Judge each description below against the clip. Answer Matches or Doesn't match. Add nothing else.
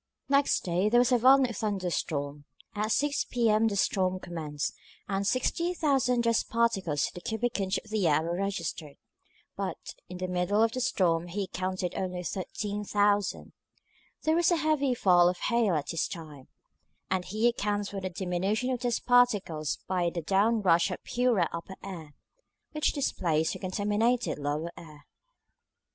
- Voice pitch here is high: Matches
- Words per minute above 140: Matches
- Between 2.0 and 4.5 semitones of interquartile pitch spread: Doesn't match